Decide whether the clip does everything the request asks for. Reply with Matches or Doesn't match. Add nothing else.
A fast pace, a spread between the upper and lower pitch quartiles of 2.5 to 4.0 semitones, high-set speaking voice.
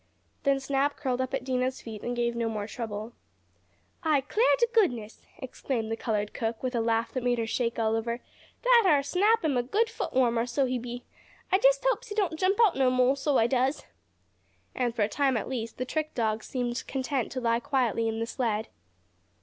Matches